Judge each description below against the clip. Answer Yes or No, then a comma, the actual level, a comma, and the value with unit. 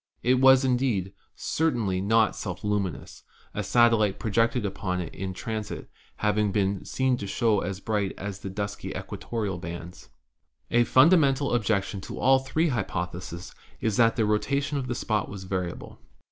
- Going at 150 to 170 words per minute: Yes, average, 160 wpm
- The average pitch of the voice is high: No, low, 105 Hz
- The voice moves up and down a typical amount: Yes, average, 4.2 semitones